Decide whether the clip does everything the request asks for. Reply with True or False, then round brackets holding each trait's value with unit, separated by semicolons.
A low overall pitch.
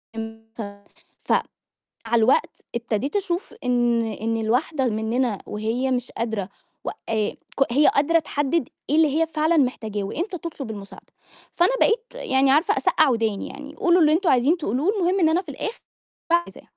False (265 Hz)